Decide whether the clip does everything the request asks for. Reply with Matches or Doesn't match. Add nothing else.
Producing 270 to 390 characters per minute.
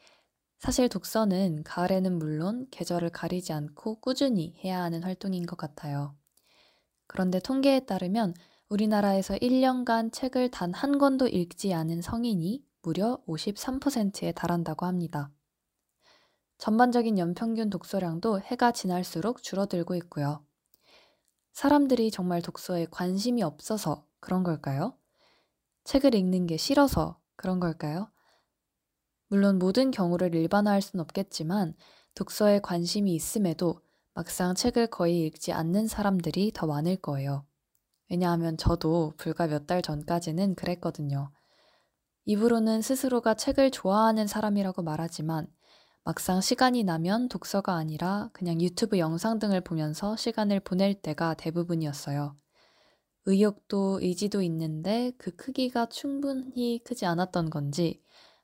Matches